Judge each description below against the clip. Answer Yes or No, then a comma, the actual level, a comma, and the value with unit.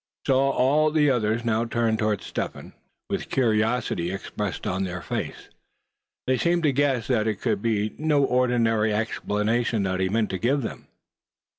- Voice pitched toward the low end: Yes, low, 115 Hz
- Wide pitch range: No, average, 3.6 semitones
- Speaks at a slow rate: No, average, 170 wpm